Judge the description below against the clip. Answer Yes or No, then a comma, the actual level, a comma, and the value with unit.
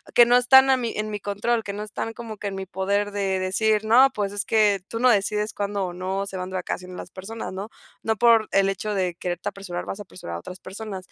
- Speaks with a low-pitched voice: No, high, 205 Hz